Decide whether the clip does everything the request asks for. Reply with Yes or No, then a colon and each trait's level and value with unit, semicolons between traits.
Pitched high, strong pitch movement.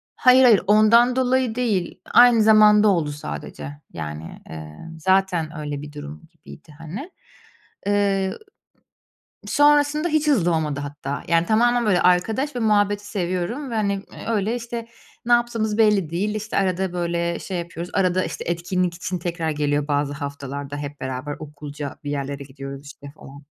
No: medium, 180 Hz; wide, 6.8 semitones